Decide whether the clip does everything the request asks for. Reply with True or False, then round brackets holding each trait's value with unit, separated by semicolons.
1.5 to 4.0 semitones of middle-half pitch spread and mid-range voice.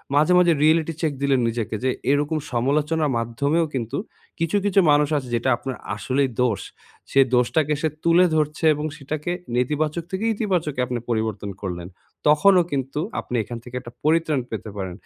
False (4.5 semitones; 145 Hz)